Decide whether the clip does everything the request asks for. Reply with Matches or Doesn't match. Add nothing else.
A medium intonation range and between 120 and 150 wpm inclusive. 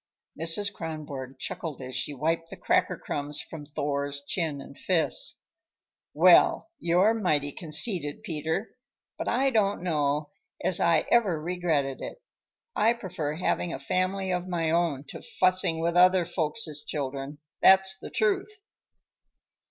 Matches